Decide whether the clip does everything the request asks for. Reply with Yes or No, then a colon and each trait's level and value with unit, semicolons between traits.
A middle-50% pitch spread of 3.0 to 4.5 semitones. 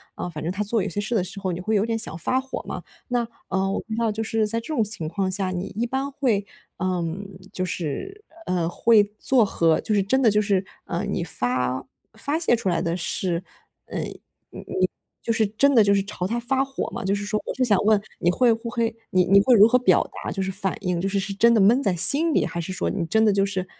Yes: average, 3.8 semitones